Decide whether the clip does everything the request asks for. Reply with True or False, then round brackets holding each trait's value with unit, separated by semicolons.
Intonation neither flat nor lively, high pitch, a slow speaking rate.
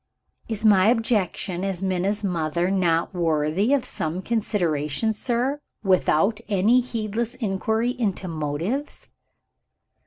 True (4.6 semitones; 195 Hz; 105 wpm)